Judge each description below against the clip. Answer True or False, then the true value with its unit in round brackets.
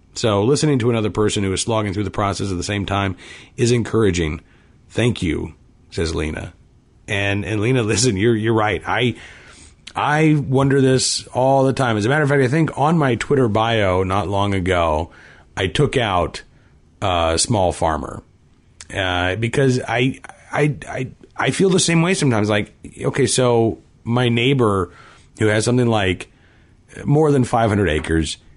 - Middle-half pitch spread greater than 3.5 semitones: True (5.2 semitones)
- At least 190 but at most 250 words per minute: False (170 wpm)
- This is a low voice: True (110 Hz)